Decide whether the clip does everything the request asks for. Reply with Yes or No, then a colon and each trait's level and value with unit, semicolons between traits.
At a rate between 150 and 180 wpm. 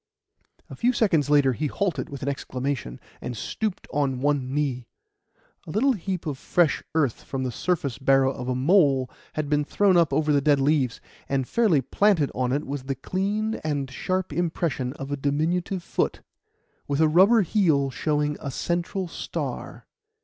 Yes: average, 170 wpm